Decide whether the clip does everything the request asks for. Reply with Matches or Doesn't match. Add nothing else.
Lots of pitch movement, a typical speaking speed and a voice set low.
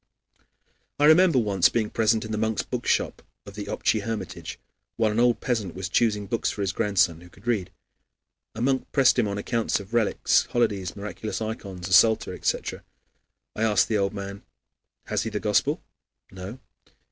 Doesn't match